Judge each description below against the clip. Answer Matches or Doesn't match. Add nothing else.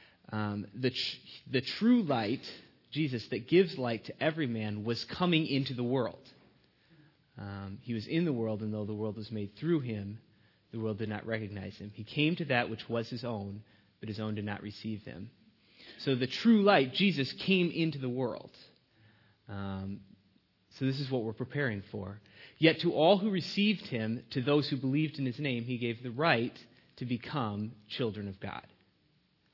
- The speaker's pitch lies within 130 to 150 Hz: Doesn't match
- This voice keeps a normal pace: Matches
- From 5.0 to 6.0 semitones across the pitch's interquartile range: Matches